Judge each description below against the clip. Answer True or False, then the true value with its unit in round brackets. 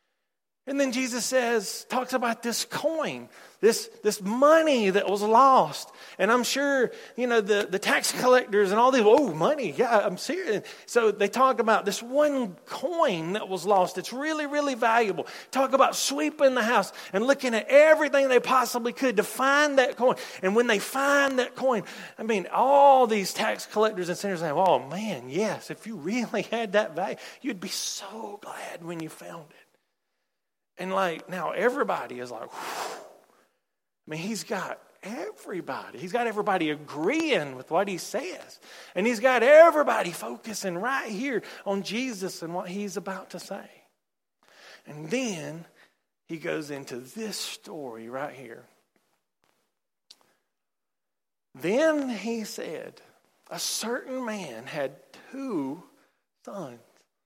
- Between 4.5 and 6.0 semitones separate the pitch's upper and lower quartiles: True (5.2 semitones)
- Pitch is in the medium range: False (230 Hz)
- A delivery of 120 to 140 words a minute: False (155 wpm)